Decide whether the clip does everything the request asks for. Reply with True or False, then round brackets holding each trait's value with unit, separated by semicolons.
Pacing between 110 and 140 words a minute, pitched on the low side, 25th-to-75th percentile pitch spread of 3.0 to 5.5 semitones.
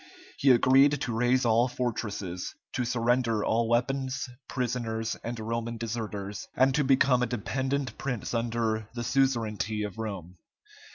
False (135 wpm; 120 Hz; 2.6 semitones)